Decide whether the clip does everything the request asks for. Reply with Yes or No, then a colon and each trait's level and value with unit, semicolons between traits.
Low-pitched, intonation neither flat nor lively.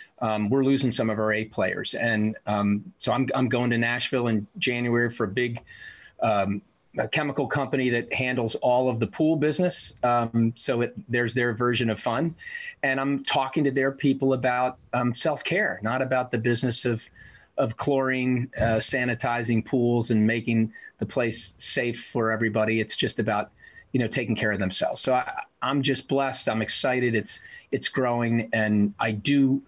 Yes: low, 120 Hz; average, 3.1 semitones